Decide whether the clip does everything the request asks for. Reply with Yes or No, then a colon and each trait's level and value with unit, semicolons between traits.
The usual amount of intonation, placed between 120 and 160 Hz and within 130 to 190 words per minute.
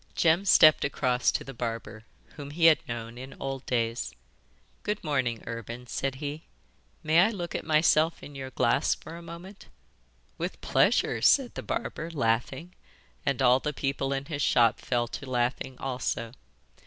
Yes: average, 4.4 semitones; low, 135 Hz; average, 165 wpm